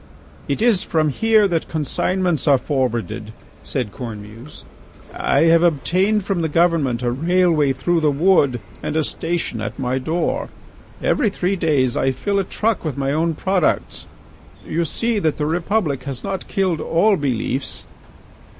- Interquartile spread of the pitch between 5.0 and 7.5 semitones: Yes, wide, 5.5 semitones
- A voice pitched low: No, medium, 160 Hz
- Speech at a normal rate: Yes, average, 155 wpm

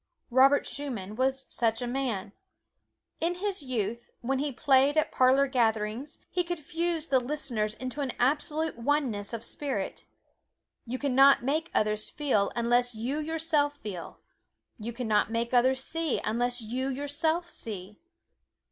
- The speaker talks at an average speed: Yes, average, 145 wpm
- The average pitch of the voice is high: Yes, very high, 260 Hz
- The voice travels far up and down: No, average, 3.9 semitones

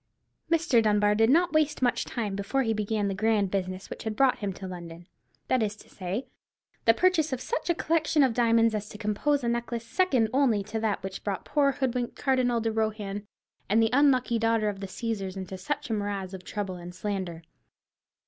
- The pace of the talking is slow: No, average, 195 wpm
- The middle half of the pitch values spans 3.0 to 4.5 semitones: Yes, average, 4.1 semitones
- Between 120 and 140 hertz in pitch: No, high, 220 Hz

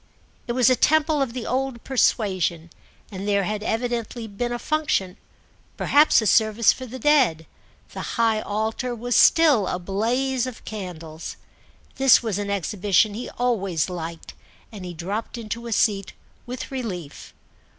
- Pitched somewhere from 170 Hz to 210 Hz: No, high, 220 Hz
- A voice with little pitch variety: No, average, 4.2 semitones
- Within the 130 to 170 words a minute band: Yes, average, 150 wpm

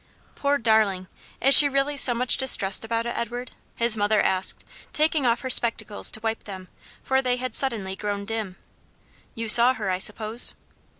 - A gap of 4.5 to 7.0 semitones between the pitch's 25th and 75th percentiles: No, average, 3.5 semitones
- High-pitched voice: Yes, high, 230 Hz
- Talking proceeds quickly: No, average, 175 wpm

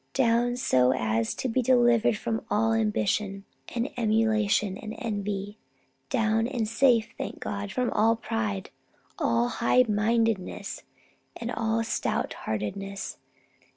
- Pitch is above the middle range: Yes, high, 220 Hz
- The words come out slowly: Yes, slow, 120 wpm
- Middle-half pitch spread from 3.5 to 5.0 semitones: No, average, 2.7 semitones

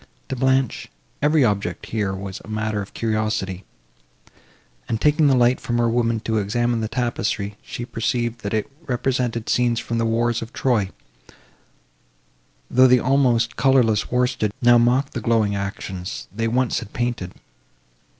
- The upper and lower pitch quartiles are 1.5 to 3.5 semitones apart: Yes, narrow, 2.5 semitones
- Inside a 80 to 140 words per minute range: No, average, 150 wpm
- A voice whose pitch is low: Yes, low, 115 Hz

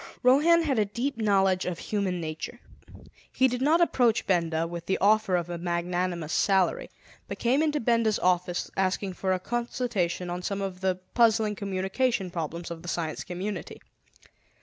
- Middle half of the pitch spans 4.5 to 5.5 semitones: Yes, average, 4.9 semitones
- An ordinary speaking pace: Yes, average, 165 wpm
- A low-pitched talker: No, high, 190 Hz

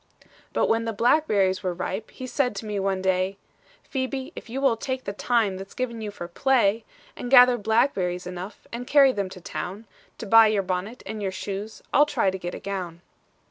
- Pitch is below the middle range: No, high, 210 Hz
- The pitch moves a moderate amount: Yes, average, 4.5 semitones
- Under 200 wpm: No, fast, 205 wpm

